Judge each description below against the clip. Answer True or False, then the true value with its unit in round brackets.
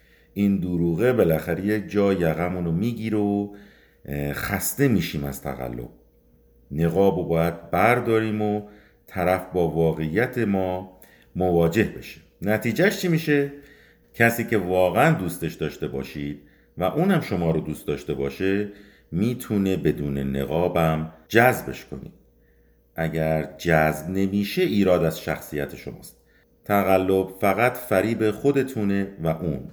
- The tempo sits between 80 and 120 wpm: True (115 wpm)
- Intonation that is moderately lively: True (4.6 semitones)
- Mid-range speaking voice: False (90 Hz)